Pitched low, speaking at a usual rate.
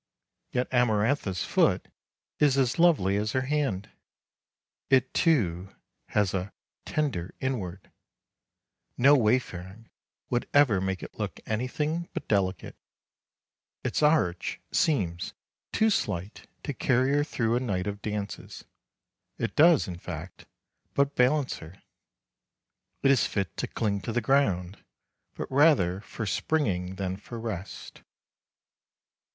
No: low, 110 Hz; slow, 125 wpm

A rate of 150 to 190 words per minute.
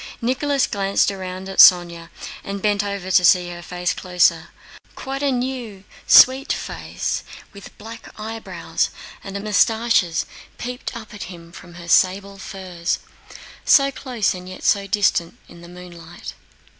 No: slow, 135 wpm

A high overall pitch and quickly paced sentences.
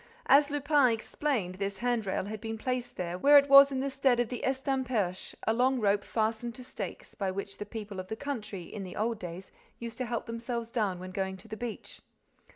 Yes: high, 230 Hz; fast, 215 wpm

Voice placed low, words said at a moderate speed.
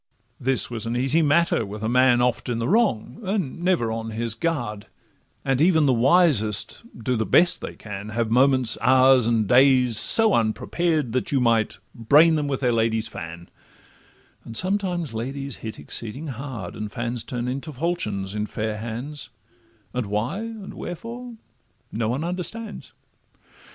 Yes: low, 125 Hz; average, 160 wpm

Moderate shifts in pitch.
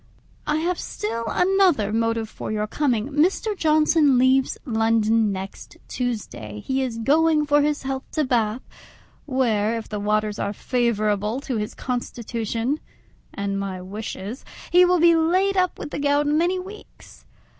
No: wide, 6.0 semitones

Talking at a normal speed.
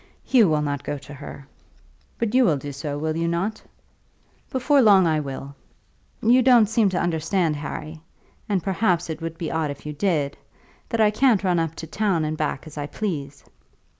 Yes: average, 195 wpm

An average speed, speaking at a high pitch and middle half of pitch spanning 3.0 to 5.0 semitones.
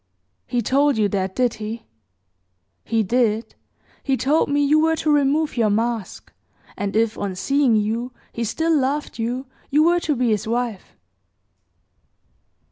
Yes: average, 150 wpm; high, 240 Hz; average, 4.7 semitones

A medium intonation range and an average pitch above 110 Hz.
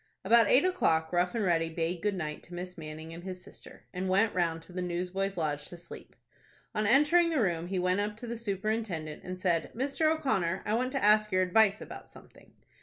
Yes: average, 4.2 semitones; medium, 185 Hz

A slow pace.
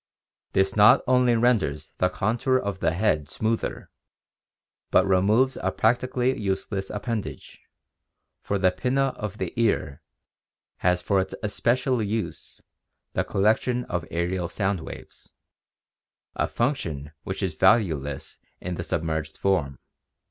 Yes: slow, 125 wpm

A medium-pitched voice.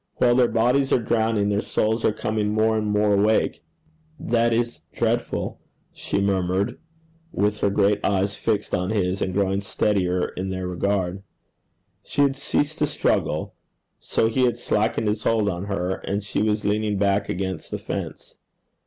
No: low, 105 Hz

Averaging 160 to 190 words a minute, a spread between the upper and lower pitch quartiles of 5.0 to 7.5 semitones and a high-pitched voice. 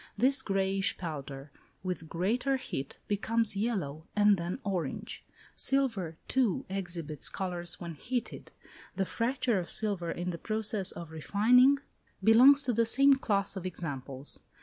No: slow, 135 wpm; wide, 5.4 semitones; high, 195 Hz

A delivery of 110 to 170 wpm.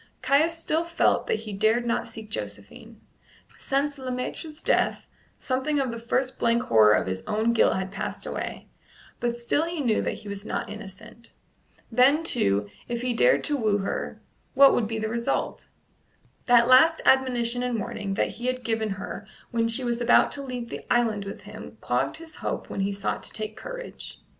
No: average, 190 wpm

